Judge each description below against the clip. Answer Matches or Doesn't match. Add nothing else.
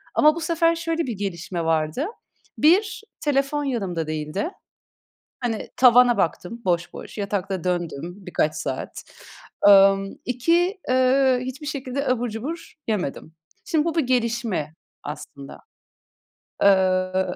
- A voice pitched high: Matches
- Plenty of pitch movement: Matches